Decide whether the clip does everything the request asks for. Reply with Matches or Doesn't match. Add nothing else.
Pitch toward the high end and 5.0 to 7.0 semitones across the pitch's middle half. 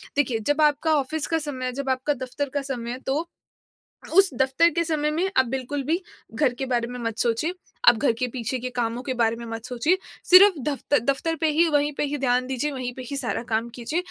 Doesn't match